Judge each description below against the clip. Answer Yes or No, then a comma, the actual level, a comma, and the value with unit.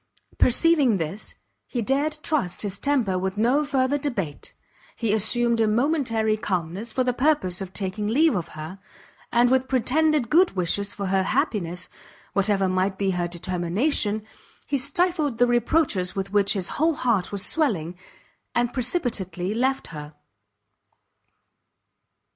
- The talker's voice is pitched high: Yes, high, 220 Hz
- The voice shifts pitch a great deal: Yes, wide, 5.9 semitones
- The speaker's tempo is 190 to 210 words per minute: No, average, 140 wpm